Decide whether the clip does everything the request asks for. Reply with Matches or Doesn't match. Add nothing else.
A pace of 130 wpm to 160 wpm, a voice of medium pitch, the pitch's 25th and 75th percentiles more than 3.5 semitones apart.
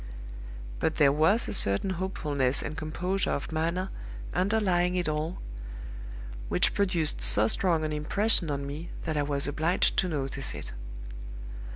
Matches